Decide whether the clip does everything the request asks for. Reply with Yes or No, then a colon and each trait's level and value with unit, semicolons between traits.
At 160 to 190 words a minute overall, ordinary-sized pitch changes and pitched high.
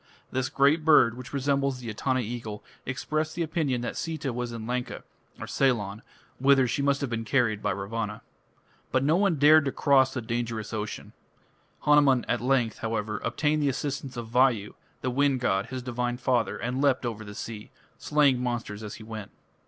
No: average, 180 wpm; average, 3.6 semitones; low, 125 Hz